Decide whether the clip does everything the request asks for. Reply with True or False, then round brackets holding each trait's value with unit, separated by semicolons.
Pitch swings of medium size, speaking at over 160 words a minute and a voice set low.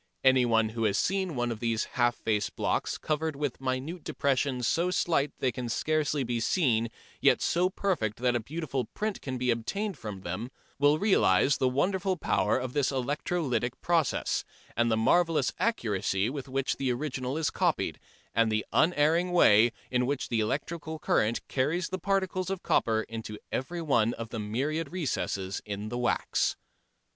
False (5.8 semitones; 170 wpm; 130 Hz)